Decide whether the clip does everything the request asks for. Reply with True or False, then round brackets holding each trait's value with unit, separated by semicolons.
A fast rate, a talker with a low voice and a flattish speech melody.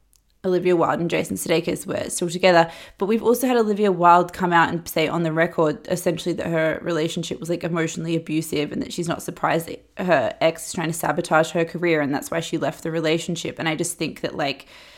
False (225 wpm; 170 Hz; 1.7 semitones)